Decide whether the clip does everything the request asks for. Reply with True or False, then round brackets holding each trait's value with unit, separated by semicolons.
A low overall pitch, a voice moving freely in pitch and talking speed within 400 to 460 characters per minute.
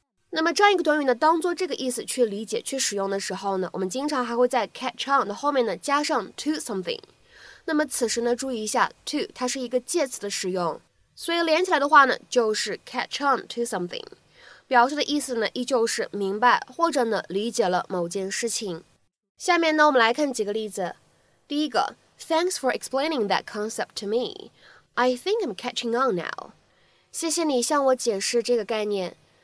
False (250 Hz; 5.8 semitones; 420 characters per minute)